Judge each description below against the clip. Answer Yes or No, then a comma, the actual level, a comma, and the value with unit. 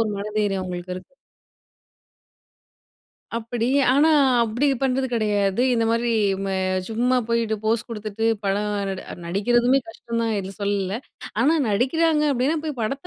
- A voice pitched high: Yes, high, 225 Hz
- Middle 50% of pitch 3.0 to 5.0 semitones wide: Yes, average, 3.7 semitones